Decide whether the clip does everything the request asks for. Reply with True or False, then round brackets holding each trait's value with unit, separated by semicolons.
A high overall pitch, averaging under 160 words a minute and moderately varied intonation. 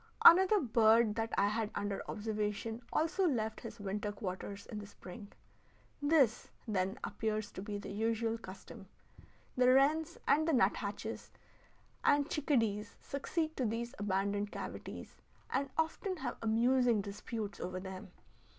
True (225 Hz; 140 wpm; 4.5 semitones)